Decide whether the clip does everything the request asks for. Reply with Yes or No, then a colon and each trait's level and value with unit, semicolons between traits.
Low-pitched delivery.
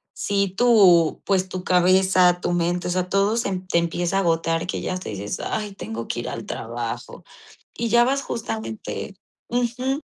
No: medium, 185 Hz